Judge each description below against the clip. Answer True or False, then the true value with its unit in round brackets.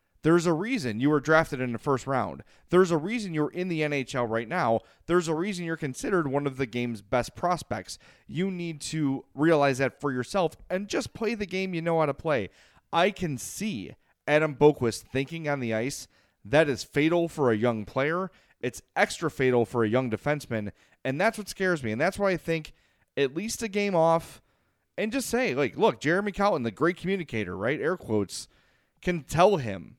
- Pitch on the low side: False (150 Hz)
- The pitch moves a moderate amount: False (5.8 semitones)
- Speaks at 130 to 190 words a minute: False (200 wpm)